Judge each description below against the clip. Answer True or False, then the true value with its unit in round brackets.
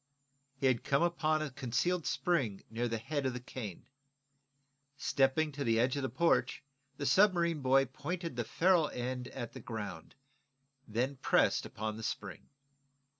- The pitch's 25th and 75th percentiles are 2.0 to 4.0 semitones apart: False (4.7 semitones)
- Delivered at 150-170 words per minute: True (160 wpm)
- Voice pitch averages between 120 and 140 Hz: True (135 Hz)